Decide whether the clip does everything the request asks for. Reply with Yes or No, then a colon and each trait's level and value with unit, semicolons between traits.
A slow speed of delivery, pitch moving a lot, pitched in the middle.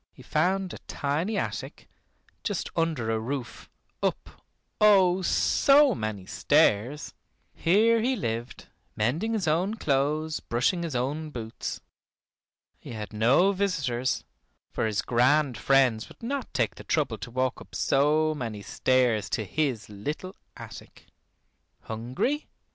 Yes: slow, 130 wpm; wide, 7.6 semitones; medium, 145 Hz